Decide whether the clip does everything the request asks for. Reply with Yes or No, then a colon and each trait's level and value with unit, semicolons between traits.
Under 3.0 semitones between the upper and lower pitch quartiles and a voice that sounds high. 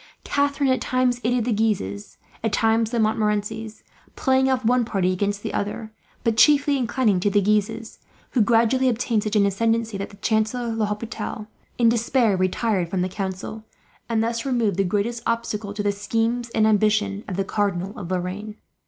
Yes: narrow, 2.4 semitones; high, 220 Hz